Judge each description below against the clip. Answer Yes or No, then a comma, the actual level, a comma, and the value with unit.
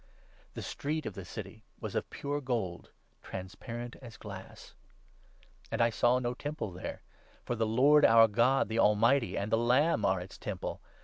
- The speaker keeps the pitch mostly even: No, average, 3.5 semitones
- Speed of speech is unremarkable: Yes, average, 175 wpm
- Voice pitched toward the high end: No, low, 115 Hz